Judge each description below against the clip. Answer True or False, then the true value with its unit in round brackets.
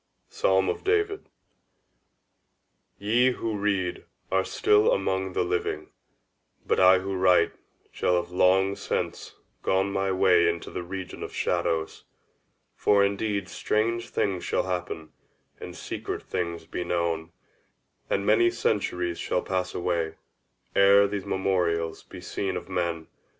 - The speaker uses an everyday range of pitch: False (2.2 semitones)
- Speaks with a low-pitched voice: True (95 Hz)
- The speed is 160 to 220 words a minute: False (135 wpm)